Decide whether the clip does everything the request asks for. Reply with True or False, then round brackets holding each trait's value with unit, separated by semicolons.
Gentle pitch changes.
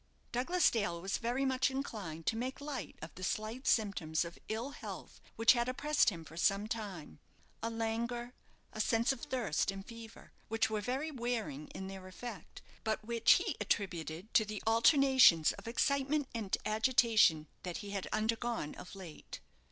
False (4.1 semitones)